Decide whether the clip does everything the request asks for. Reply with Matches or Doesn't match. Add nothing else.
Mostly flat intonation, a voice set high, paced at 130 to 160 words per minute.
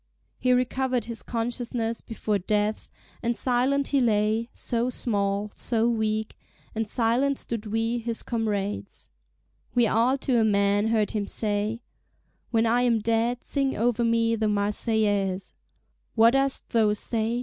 Matches